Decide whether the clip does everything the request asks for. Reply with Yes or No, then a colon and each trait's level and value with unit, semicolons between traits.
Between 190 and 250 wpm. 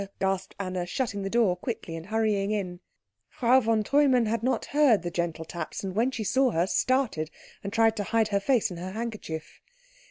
Yes: average, 195 wpm